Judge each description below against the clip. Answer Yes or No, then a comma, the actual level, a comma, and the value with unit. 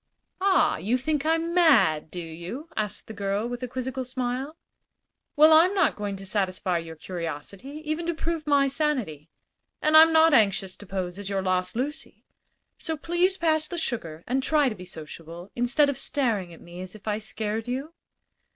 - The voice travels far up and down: Yes, wide, 8.5 semitones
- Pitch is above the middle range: Yes, high, 245 Hz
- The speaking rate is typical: Yes, average, 185 wpm